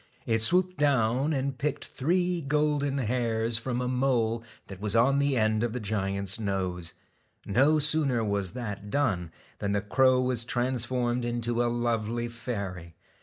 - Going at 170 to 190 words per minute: No, average, 155 wpm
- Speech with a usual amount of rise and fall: Yes, average, 3.9 semitones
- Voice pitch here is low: Yes, low, 120 Hz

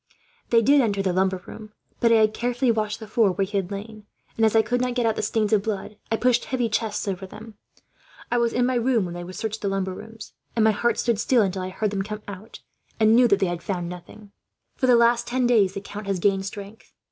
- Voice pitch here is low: No, high, 215 Hz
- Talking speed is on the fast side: Yes, fast, 260 wpm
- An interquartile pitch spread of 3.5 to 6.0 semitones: No, average, 3.0 semitones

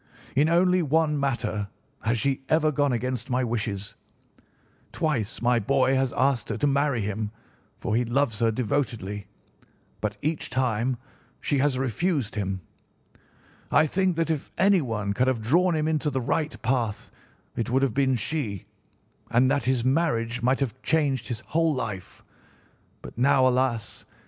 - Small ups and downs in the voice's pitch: No, average, 4.1 semitones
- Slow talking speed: No, average, 155 wpm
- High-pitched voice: No, low, 130 Hz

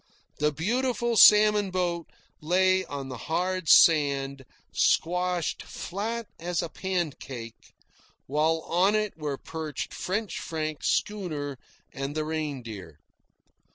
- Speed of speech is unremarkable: No, slow, 110 wpm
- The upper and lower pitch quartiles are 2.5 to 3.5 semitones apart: No, average, 4.5 semitones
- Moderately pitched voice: Yes, medium, 165 Hz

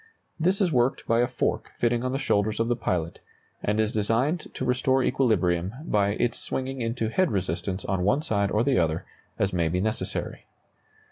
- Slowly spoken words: No, average, 190 wpm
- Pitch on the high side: No, low, 115 Hz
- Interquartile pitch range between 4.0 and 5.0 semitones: Yes, average, 4.5 semitones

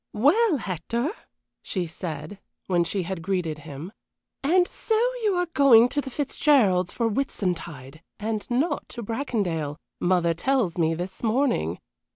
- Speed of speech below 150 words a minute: Yes, average, 140 wpm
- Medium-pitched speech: No, high, 195 Hz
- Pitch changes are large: Yes, wide, 8.2 semitones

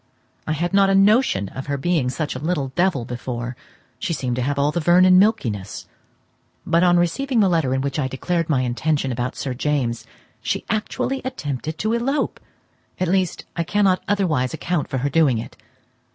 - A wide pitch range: Yes, wide, 6.0 semitones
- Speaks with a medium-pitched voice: Yes, medium, 155 Hz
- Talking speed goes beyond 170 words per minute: Yes, average, 185 wpm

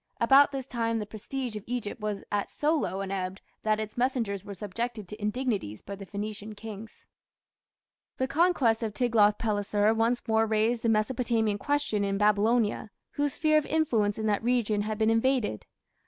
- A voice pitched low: No, high, 220 Hz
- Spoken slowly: No, average, 175 wpm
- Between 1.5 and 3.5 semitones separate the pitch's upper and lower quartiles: Yes, average, 2.9 semitones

